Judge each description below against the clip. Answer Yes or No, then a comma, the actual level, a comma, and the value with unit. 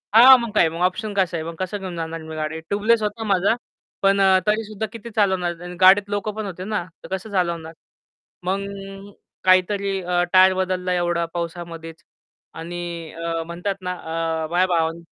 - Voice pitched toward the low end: No, medium, 185 Hz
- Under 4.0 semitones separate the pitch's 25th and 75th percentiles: Yes, average, 2.7 semitones